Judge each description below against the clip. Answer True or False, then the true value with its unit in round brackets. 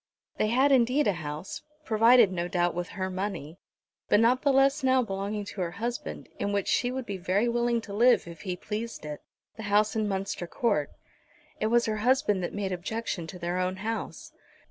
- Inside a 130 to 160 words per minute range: False (200 wpm)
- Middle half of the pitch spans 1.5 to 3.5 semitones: False (4.5 semitones)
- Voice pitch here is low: False (210 Hz)